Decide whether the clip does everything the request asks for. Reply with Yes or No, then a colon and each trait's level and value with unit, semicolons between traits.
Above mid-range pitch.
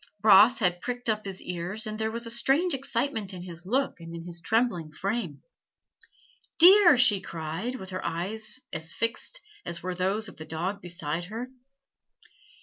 Yes: high, 200 Hz